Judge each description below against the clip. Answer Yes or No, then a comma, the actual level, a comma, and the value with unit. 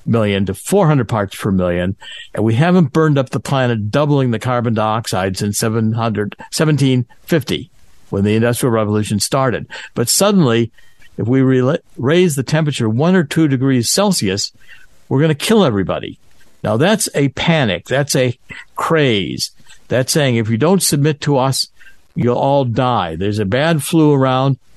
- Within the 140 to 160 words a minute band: Yes, average, 155 wpm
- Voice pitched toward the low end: Yes, low, 130 Hz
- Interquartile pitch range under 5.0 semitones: No, wide, 5.6 semitones